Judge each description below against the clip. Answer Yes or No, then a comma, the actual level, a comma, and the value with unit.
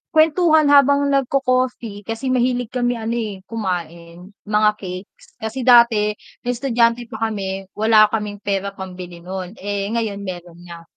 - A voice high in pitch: Yes, high, 215 Hz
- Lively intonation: No, average, 4.2 semitones